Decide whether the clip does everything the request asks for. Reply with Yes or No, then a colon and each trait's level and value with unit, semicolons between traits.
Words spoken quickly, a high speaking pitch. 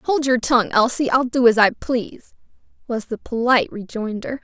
No: average, 175 wpm; high, 240 Hz